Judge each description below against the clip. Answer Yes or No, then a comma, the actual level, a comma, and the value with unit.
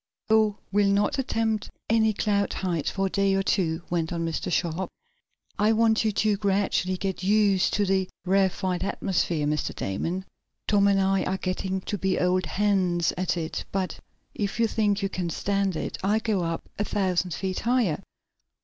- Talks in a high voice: Yes, high, 195 Hz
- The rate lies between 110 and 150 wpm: No, average, 180 wpm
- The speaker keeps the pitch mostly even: Yes, narrow, 2.1 semitones